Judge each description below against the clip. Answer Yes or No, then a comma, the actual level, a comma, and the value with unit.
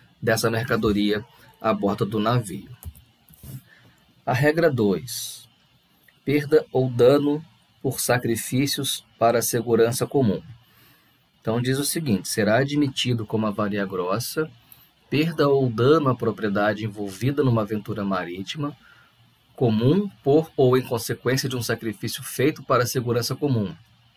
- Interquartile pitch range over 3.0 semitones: Yes, average, 3.7 semitones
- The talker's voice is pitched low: Yes, low, 120 Hz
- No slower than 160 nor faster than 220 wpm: No, slow, 120 wpm